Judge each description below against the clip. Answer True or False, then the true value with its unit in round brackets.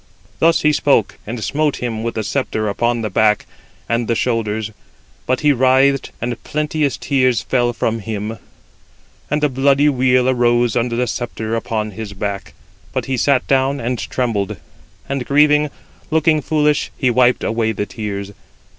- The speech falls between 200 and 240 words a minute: False (160 wpm)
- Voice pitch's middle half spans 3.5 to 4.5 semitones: True (3.8 semitones)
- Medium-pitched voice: False (120 Hz)